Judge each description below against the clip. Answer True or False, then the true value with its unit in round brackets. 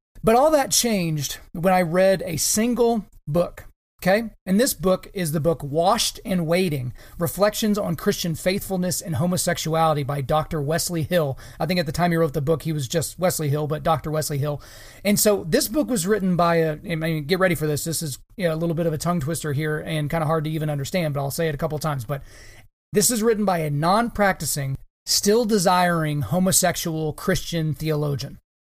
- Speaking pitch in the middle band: True (165 Hz)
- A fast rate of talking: True (215 wpm)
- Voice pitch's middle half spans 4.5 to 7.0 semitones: False (3.5 semitones)